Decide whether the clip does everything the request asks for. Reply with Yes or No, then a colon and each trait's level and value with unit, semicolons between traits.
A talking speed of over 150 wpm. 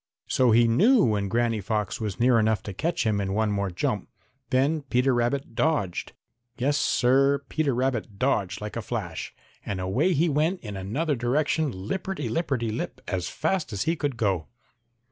Yes: average, 175 wpm